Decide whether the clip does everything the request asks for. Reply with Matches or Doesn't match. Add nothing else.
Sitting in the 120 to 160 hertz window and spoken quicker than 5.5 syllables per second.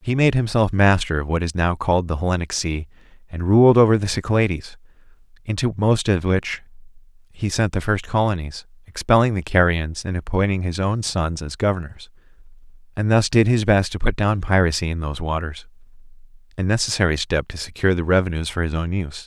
Doesn't match